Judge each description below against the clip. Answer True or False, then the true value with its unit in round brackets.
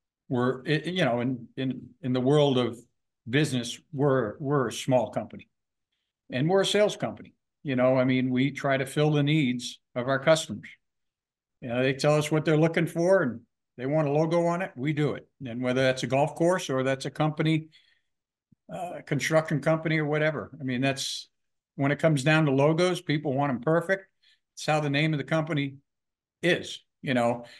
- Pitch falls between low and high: True (145 Hz)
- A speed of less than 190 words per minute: False (195 wpm)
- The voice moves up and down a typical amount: True (3.5 semitones)